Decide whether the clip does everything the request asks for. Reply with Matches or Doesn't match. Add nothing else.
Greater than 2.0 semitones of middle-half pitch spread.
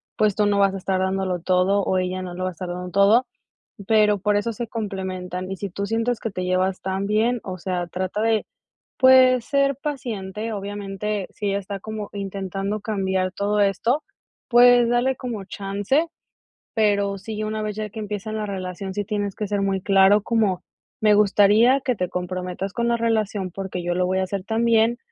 Matches